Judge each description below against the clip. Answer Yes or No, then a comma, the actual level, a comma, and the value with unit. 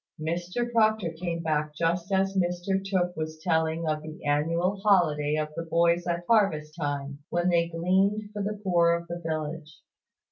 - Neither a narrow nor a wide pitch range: Yes, average, 3.0 semitones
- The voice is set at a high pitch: No, medium, 170 Hz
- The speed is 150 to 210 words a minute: Yes, average, 170 wpm